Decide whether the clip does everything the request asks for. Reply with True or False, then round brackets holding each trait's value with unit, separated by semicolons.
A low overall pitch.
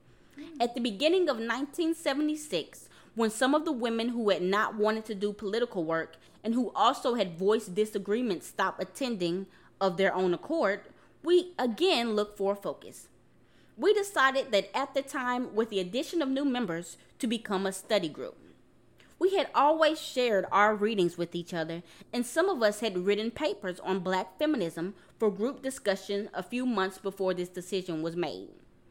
False (215 Hz)